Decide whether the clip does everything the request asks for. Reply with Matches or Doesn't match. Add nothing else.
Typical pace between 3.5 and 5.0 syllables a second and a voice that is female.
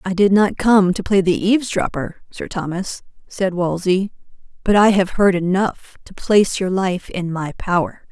Matches